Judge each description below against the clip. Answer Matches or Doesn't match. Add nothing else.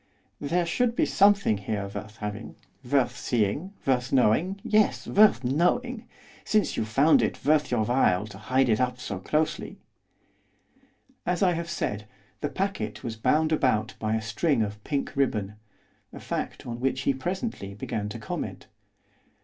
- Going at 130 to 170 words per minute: Matches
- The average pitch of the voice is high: Doesn't match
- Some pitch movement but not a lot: Doesn't match